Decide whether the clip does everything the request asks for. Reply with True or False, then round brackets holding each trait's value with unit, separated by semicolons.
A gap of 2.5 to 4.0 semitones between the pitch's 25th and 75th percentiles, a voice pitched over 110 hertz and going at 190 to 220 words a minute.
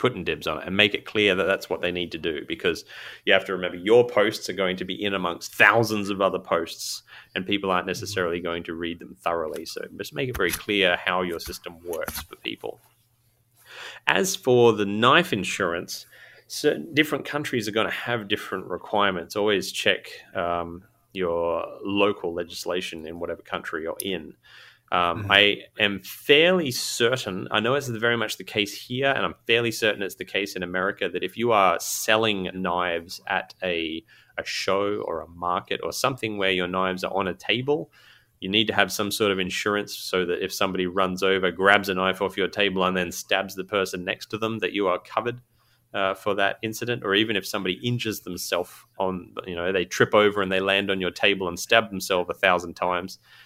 False (3.3 semitones; 100 Hz; 205 wpm)